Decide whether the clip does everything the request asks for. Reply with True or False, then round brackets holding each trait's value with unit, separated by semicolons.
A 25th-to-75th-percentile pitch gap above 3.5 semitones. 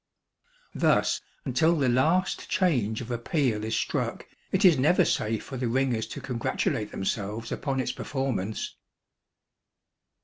True (4.6 semitones)